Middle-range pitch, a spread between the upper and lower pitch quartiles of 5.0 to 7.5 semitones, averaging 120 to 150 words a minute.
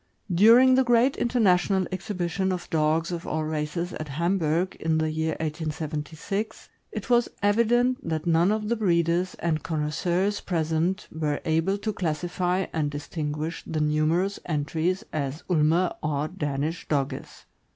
No: medium, 170 Hz; average, 3.6 semitones; average, 145 wpm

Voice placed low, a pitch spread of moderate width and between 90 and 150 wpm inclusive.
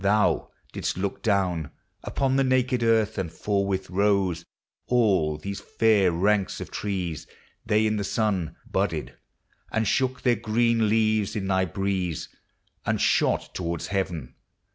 Yes: low, 100 Hz; average, 3.0 semitones; average, 140 wpm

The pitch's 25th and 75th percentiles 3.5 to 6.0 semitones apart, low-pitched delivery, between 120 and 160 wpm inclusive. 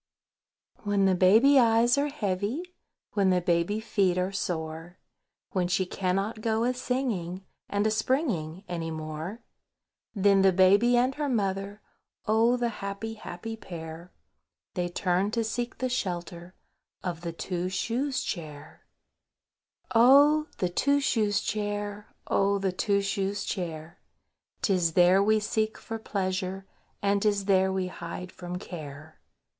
No: average, 3.8 semitones; high, 195 Hz; average, 140 wpm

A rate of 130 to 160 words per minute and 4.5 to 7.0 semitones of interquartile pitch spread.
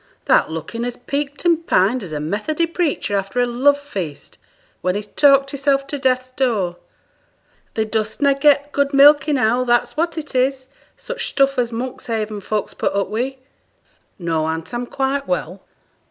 No: average, 170 wpm; average, 5.1 semitones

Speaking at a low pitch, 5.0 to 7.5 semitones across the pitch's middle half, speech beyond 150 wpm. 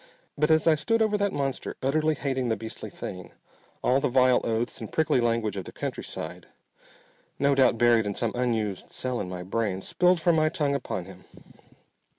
Yes: low, 125 Hz; wide, 5.6 semitones; average, 185 wpm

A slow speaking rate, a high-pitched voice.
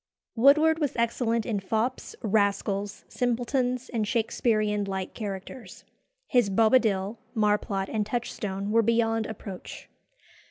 Yes: slow, 110 wpm; high, 220 Hz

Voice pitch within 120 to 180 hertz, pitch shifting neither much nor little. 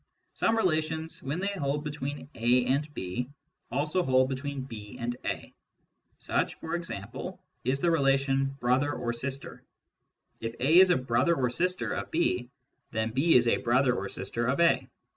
Yes: low, 135 Hz; average, 4.3 semitones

